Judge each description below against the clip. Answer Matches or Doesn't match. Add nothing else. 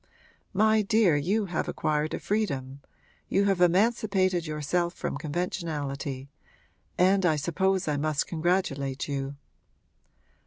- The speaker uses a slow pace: Matches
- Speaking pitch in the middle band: Matches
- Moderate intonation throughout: Matches